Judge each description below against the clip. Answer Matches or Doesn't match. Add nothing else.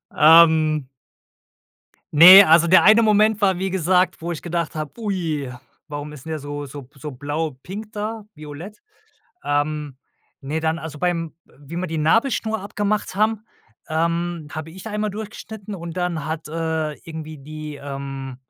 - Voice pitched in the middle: Matches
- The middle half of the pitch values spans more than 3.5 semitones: Matches